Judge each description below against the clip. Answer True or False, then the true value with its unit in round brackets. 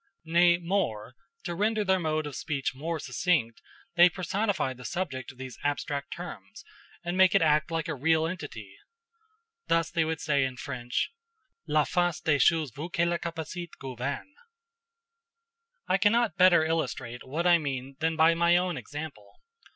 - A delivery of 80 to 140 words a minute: False (160 wpm)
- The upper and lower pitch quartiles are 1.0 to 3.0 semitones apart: False (4.1 semitones)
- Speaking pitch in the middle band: True (160 Hz)